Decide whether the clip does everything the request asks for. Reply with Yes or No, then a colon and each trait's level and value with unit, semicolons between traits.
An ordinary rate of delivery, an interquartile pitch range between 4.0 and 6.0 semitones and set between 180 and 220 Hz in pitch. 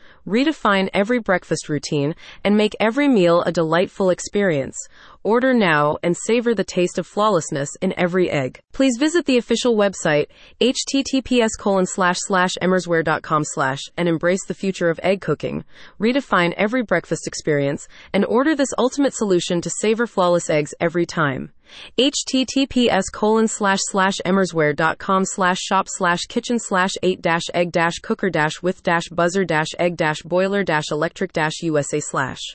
Yes: average, 150 wpm; average, 4.3 semitones; medium, 185 Hz